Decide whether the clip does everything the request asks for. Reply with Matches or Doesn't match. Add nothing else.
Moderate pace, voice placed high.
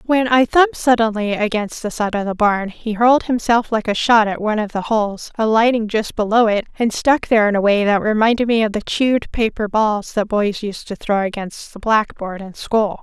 Doesn't match